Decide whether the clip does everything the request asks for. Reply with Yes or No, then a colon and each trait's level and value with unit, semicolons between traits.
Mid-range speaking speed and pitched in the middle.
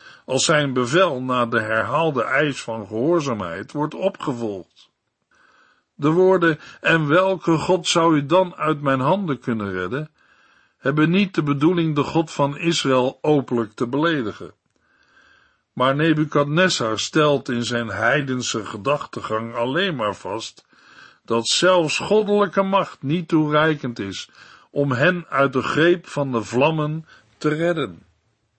No: slow, 130 wpm; medium, 145 Hz